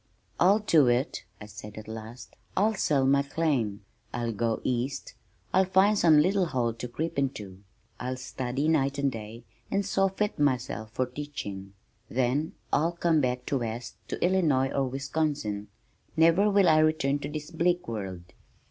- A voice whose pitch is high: No, medium, 140 Hz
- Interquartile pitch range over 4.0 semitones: Yes, wide, 5.5 semitones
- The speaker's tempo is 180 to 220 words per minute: No, average, 160 wpm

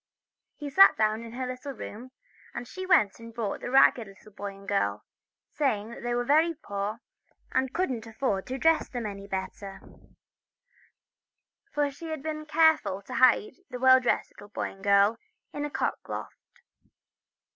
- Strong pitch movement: Yes, wide, 5.9 semitones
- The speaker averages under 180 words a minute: Yes, average, 160 wpm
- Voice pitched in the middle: No, high, 240 Hz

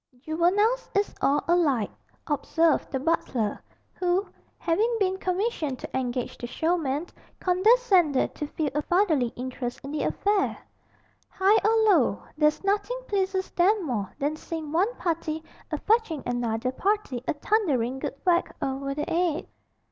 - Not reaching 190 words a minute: Yes, average, 140 wpm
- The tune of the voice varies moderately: No, wide, 6.0 semitones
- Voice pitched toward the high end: Yes, very high, 330 Hz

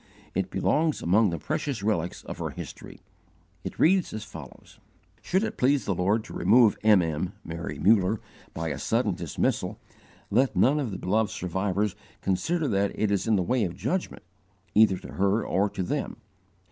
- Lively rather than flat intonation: No, average, 4.2 semitones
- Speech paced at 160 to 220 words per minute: Yes, average, 175 wpm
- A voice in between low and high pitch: No, low, 105 Hz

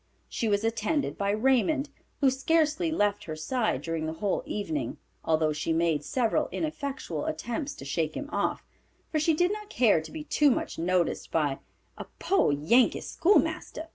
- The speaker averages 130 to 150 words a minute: No, average, 170 wpm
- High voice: Yes, high, 225 Hz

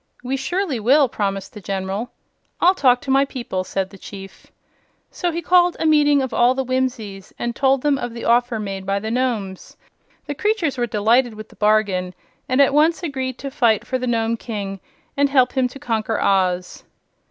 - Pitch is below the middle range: No, high, 245 Hz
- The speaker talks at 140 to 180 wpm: No, average, 195 wpm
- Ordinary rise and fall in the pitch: Yes, average, 4.8 semitones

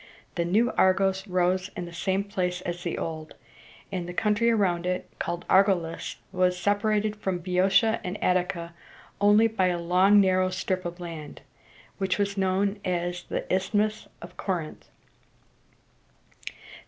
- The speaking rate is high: No, average, 150 wpm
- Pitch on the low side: No, medium, 185 Hz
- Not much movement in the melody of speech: Yes, narrow, 2.2 semitones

